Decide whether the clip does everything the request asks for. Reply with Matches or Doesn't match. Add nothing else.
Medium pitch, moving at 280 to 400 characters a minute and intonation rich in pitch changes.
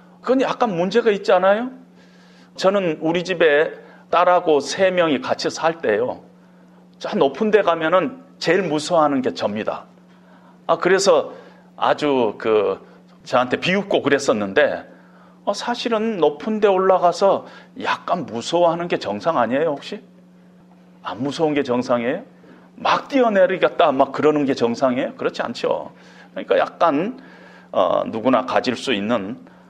Doesn't match